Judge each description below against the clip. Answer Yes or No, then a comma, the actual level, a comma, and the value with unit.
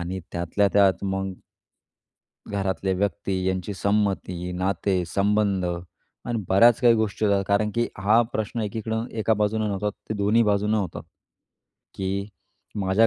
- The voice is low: Yes, low, 100 Hz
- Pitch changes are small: Yes, narrow, 2.1 semitones